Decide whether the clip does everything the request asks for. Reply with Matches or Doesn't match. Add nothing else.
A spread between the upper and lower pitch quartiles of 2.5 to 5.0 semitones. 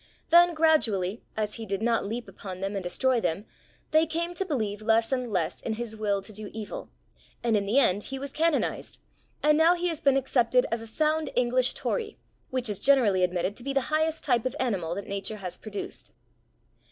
Doesn't match